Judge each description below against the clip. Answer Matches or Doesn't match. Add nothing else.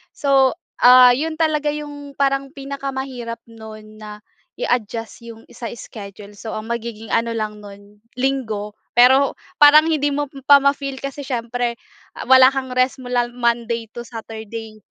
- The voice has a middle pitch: Doesn't match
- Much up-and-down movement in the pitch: Doesn't match